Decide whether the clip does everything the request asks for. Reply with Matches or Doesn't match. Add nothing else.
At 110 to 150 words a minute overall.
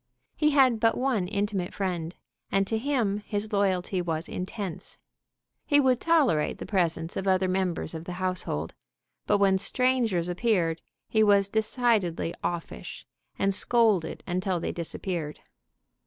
Matches